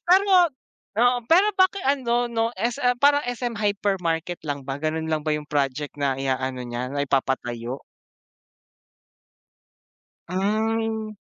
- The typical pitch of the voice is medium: No, high, 200 Hz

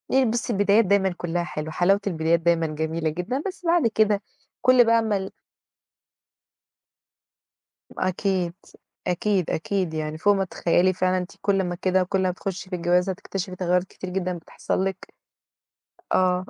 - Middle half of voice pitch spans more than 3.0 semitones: No, narrow, 2.4 semitones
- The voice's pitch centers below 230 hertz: Yes, medium, 185 Hz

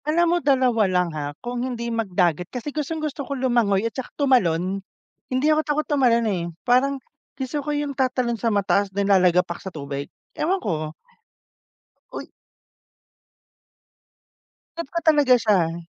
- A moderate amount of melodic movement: No, wide, 6.9 semitones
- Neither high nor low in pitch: No, high, 240 Hz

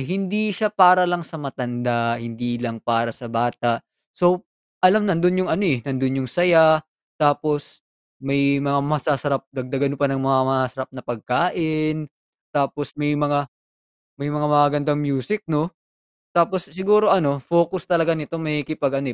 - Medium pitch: Yes, medium, 145 Hz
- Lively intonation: No, average, 4.3 semitones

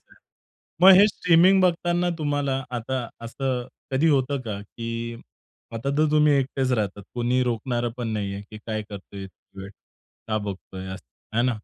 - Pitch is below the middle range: Yes, low, 125 Hz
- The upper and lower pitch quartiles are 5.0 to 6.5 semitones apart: Yes, average, 5.3 semitones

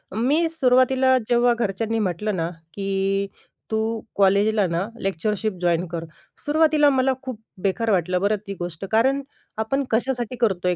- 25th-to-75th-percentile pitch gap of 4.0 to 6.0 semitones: Yes, average, 4.8 semitones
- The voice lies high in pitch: Yes, high, 220 Hz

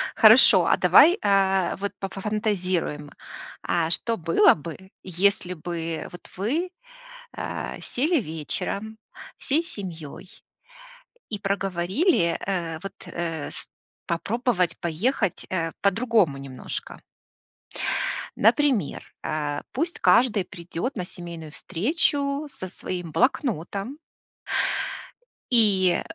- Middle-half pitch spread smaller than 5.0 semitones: No, average, 5.3 semitones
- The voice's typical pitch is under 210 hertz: Yes, high, 190 Hz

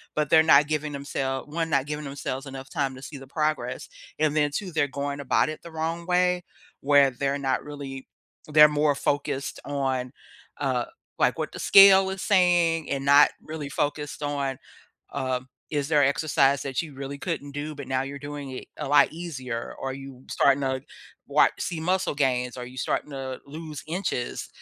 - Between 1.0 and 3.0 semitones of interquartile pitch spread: Yes, narrow, 2.4 semitones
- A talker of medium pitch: Yes, medium, 145 Hz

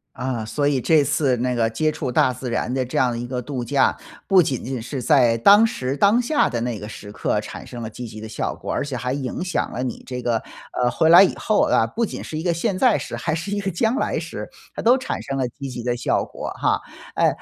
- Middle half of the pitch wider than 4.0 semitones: Yes, average, 5.3 semitones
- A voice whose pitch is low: Yes, low, 130 Hz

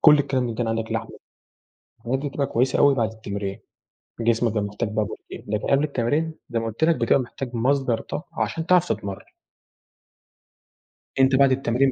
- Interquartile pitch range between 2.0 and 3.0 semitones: No, average, 3.7 semitones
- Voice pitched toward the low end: Yes, low, 125 Hz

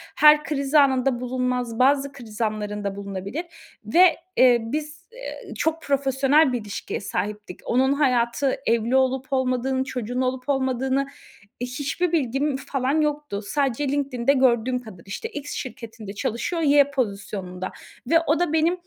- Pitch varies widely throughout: No, average, 3.6 semitones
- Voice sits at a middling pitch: No, very high, 260 Hz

